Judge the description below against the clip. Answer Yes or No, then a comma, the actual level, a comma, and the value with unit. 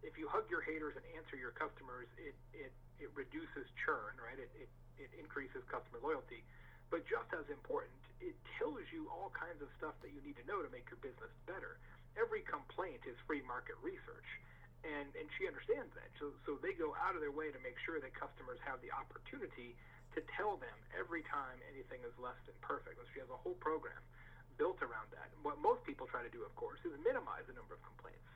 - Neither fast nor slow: No, fast, 220 wpm